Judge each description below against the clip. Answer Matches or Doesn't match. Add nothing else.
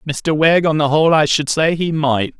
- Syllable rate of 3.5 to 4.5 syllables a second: Doesn't match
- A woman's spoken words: Doesn't match